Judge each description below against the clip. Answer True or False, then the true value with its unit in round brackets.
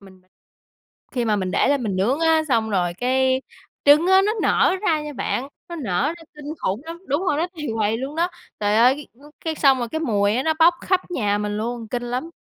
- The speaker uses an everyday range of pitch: False (6.7 semitones)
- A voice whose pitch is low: False (260 Hz)